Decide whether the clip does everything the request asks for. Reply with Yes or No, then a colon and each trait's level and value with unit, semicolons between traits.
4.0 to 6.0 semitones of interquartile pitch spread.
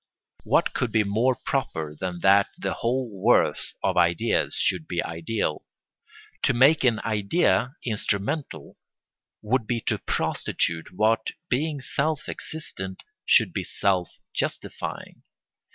Yes: wide, 5.6 semitones